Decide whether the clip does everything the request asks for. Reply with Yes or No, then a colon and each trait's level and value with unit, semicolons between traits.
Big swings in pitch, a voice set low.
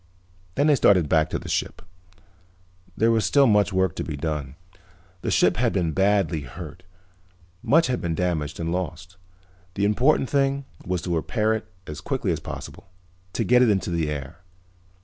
Yes: wide, 5.9 semitones; very low, 90 Hz